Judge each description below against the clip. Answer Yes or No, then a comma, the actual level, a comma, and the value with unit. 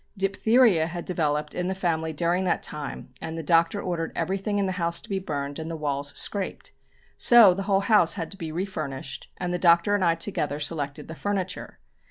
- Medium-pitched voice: Yes, medium, 170 Hz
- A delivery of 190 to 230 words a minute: Yes, fast, 205 wpm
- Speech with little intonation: No, average, 3.3 semitones